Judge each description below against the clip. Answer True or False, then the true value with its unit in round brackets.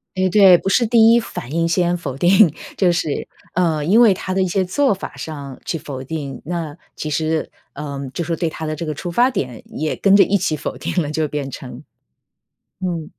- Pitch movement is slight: False (3.8 semitones)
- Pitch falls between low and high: True (170 Hz)